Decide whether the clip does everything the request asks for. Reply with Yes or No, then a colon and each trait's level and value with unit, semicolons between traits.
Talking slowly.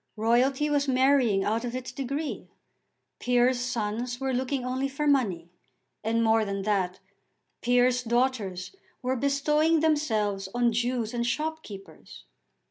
Yes: slow, 130 wpm